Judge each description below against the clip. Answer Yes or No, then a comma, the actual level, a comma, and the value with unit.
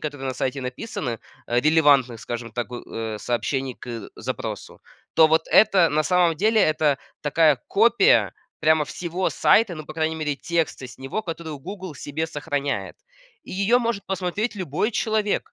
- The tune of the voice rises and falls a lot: Yes, wide, 5.7 semitones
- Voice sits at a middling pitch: Yes, medium, 155 Hz